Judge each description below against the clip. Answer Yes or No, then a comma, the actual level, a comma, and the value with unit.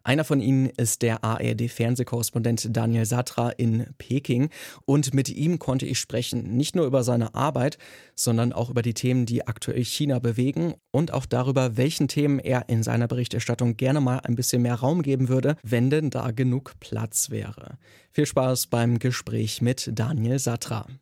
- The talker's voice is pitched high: No, low, 125 Hz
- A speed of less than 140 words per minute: No, average, 170 wpm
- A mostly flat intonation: Yes, narrow, 2.3 semitones